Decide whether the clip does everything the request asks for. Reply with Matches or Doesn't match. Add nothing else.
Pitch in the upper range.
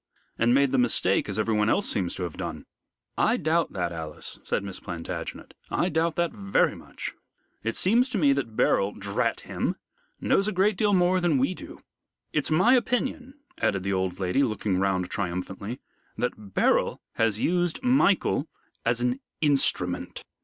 Doesn't match